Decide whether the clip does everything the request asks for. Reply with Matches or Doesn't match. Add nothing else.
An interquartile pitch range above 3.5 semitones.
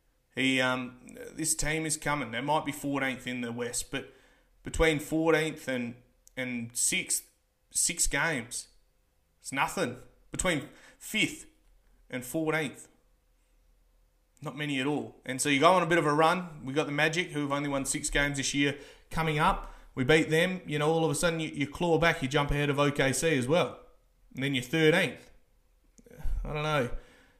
Doesn't match